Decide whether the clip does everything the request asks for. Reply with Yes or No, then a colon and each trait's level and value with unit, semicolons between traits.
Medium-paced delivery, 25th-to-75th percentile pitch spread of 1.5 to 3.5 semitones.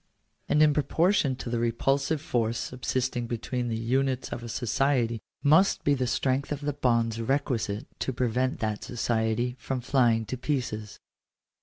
Yes: average, 160 wpm; average, 2.9 semitones